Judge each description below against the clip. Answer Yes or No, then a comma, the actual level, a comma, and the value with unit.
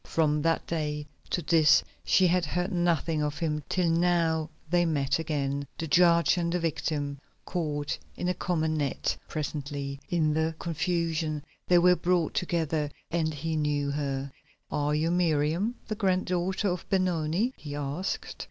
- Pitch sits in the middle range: Yes, medium, 160 Hz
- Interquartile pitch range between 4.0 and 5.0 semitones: No, average, 2.8 semitones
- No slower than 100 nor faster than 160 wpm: Yes, average, 155 wpm